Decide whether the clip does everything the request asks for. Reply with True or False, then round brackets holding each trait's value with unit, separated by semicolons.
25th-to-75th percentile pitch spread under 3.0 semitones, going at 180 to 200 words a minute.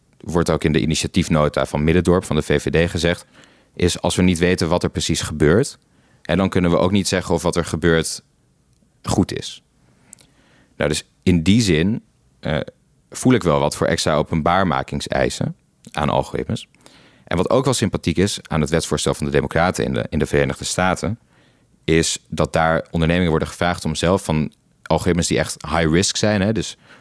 True (2.6 semitones; 185 wpm)